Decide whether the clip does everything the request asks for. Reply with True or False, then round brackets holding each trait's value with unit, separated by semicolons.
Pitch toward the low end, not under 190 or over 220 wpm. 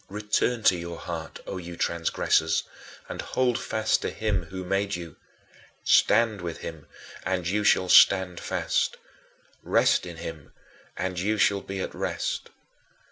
False (95 Hz; 145 wpm)